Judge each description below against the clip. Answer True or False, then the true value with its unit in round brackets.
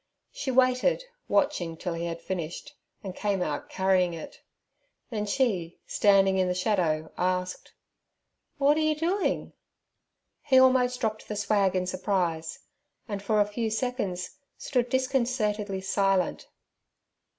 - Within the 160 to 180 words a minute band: False (135 wpm)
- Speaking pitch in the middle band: False (200 Hz)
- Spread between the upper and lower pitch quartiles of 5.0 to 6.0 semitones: True (5.5 semitones)